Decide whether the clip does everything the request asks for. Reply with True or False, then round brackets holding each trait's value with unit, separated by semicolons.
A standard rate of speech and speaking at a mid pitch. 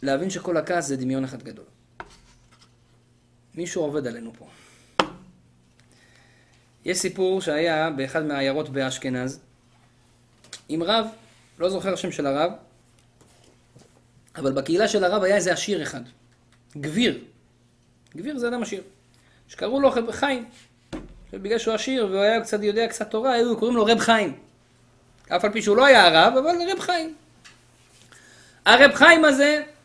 True (135 wpm; 180 Hz)